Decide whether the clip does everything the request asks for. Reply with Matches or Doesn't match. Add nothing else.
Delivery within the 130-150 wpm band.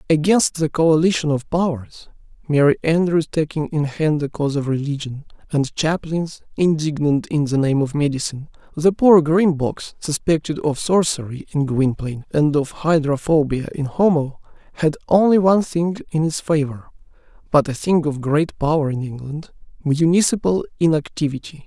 Matches